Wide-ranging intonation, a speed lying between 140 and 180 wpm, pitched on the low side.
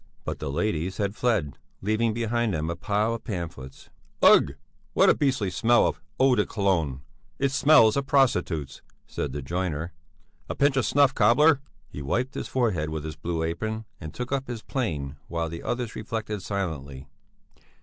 Yes: wide, 7.0 semitones; average, 170 wpm; low, 105 Hz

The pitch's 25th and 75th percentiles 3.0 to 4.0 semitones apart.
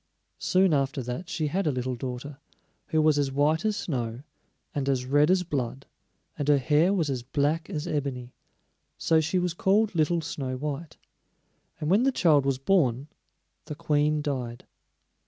Yes: average, 3.7 semitones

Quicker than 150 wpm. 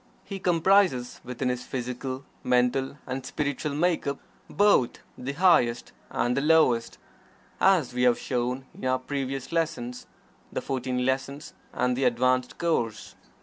No: average, 140 wpm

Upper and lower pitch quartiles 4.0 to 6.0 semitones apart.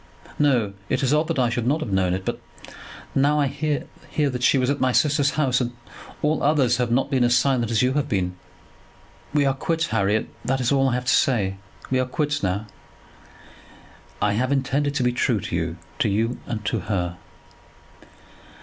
Yes: average, 4.3 semitones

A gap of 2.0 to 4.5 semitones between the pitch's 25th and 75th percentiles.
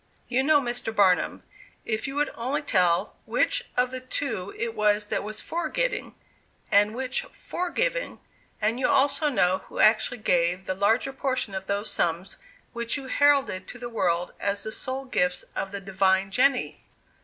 No: wide, 5.5 semitones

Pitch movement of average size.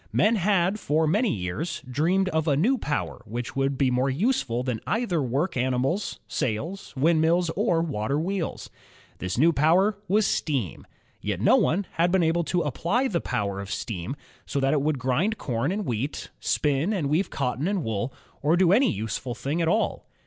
No: wide, 6.6 semitones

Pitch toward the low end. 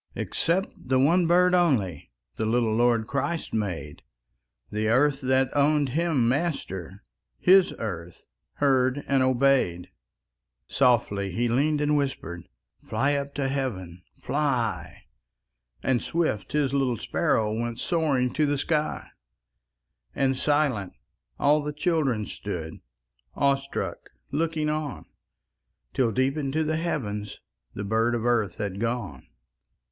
Yes: low, 130 Hz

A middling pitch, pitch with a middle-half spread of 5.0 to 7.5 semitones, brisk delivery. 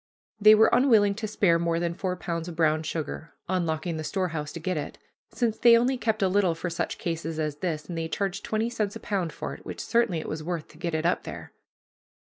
No: medium, 175 Hz; average, 4.2 semitones; fast, 235 wpm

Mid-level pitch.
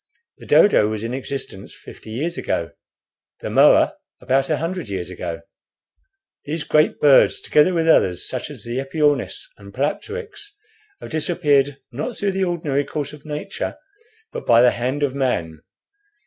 Yes: medium, 145 Hz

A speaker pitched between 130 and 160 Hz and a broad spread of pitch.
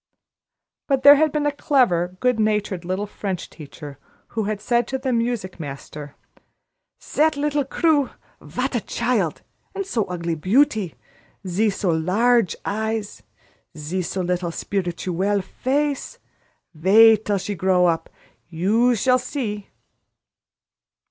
No: high, 210 Hz; wide, 5.7 semitones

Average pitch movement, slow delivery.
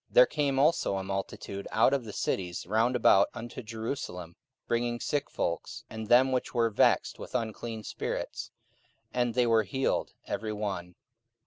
No: average, 4.0 semitones; average, 160 wpm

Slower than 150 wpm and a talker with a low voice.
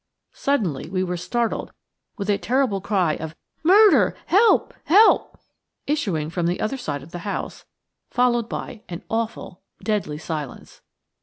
No: average, 140 wpm; high, 200 Hz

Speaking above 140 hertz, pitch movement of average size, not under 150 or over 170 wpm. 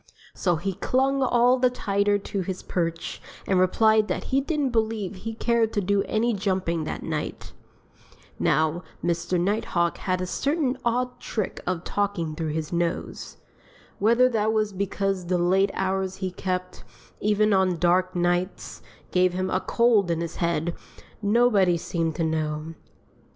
Yes: high, 190 Hz; average, 3.8 semitones; average, 155 wpm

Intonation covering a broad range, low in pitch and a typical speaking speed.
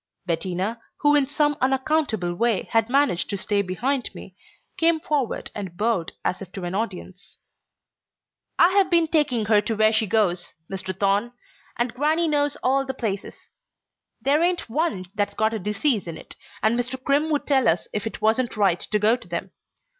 No: wide, 6.2 semitones; high, 225 Hz; average, 180 wpm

